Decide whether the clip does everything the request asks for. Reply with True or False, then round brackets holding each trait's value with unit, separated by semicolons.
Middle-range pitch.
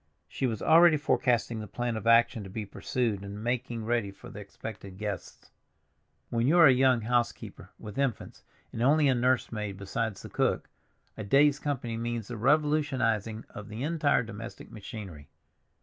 False (115 Hz)